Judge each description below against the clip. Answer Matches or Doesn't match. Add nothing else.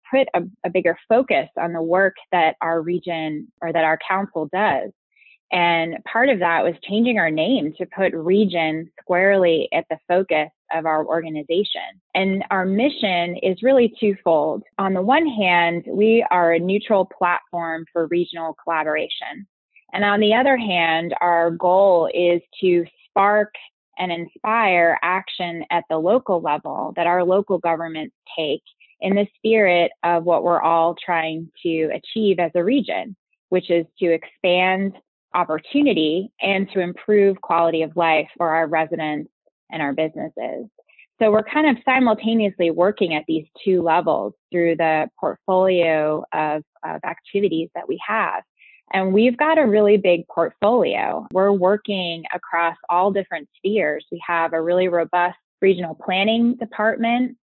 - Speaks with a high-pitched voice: Doesn't match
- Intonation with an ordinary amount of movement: Matches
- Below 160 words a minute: Matches